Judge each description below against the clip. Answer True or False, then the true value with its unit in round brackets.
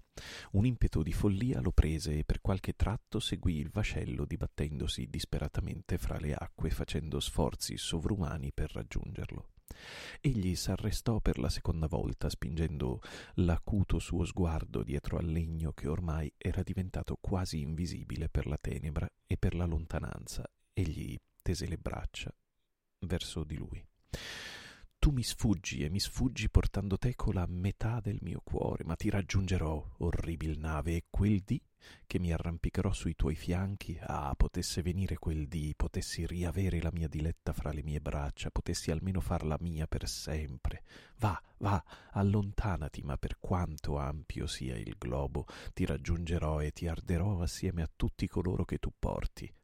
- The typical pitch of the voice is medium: False (85 Hz)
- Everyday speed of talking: True (150 wpm)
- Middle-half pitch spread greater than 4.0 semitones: False (3.6 semitones)